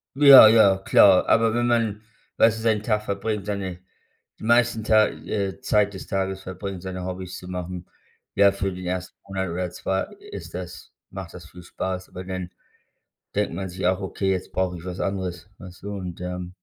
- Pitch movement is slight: Yes, narrow, 2.2 semitones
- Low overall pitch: Yes, very low, 95 Hz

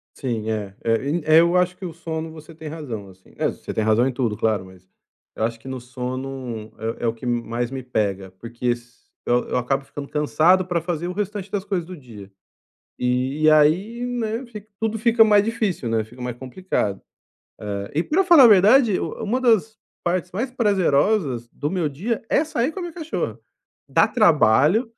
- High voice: No, medium, 155 Hz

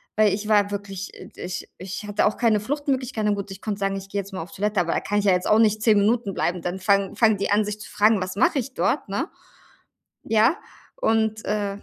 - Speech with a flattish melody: Yes, narrow, 1.9 semitones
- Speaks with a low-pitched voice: No, high, 205 Hz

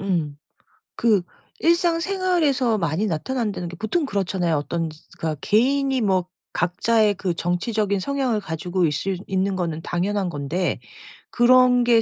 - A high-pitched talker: Yes, high, 200 Hz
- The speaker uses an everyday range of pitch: No, wide, 6.0 semitones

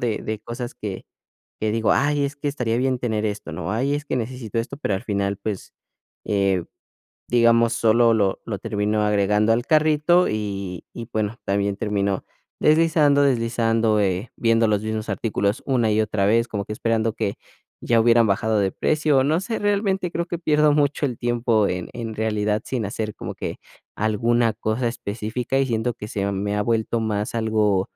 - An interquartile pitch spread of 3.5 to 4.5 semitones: No, average, 3.0 semitones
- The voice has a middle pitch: No, low, 115 Hz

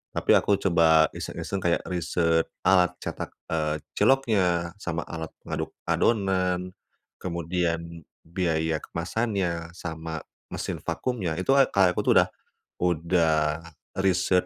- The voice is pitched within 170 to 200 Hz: No, very low, 85 Hz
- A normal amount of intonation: No, narrow, 2.1 semitones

